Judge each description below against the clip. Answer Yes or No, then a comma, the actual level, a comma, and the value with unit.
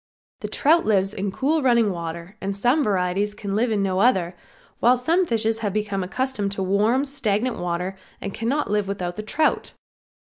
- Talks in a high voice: Yes, high, 210 Hz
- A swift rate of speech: No, average, 180 wpm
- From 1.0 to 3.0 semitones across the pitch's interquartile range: No, average, 4.2 semitones